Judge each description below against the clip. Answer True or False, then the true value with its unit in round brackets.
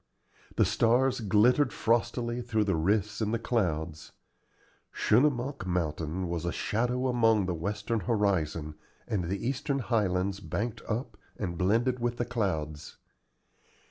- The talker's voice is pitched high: False (105 Hz)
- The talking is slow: True (130 wpm)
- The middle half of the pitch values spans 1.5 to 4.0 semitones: False (4.9 semitones)